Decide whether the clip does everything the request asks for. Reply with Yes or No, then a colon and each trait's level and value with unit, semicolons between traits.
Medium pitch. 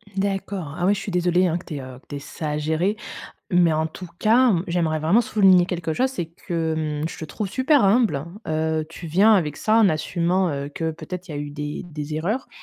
Yes: medium, 170 Hz